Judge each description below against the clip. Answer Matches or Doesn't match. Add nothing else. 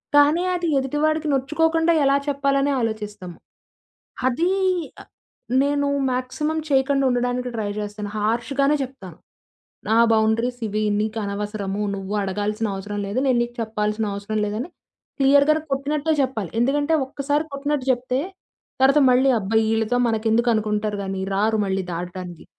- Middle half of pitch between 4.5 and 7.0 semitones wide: Matches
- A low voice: Doesn't match